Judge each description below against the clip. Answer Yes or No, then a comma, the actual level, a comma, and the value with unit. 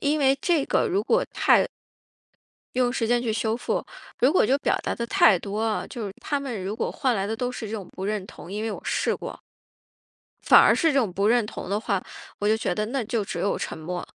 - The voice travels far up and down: No, average, 3.7 semitones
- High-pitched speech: Yes, high, 225 Hz